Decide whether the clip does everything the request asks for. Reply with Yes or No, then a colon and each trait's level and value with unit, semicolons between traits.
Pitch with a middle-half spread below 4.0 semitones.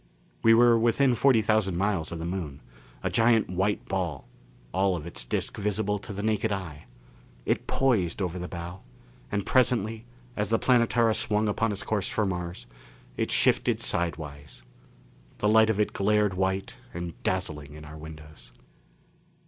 No: average, 4.3 semitones